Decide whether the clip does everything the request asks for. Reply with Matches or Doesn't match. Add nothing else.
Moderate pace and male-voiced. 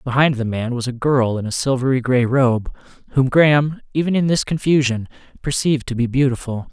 Matches